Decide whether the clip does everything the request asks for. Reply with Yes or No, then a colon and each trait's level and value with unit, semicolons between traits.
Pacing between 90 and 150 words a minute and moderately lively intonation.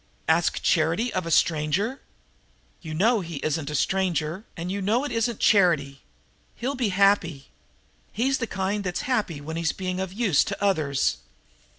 No: average, 165 wpm; average, 4.7 semitones